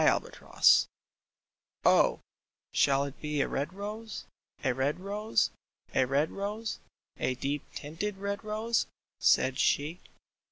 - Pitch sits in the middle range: Yes, medium, 170 Hz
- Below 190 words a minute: Yes, slow, 135 wpm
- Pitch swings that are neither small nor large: No, wide, 6.9 semitones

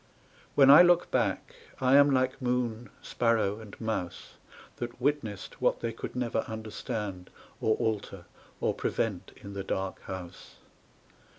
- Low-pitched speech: Yes, low, 110 Hz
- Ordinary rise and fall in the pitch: Yes, average, 4.1 semitones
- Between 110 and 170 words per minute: Yes, slow, 135 wpm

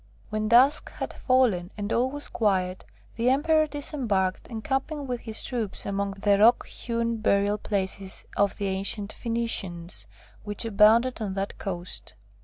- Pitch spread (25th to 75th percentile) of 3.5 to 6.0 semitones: Yes, average, 3.8 semitones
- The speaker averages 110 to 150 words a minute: Yes, average, 145 wpm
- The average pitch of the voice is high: Yes, high, 215 Hz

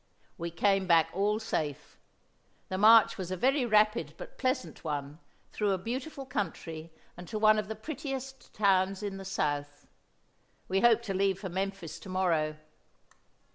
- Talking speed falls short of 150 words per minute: No, average, 160 wpm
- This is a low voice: No, high, 195 Hz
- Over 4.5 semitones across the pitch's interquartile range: No, average, 4.1 semitones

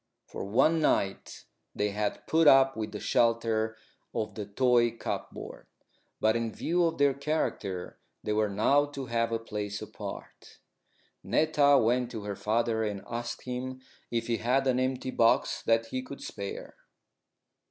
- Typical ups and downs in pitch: Yes, average, 3.3 semitones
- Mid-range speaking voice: No, low, 115 Hz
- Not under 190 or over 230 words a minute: No, average, 155 wpm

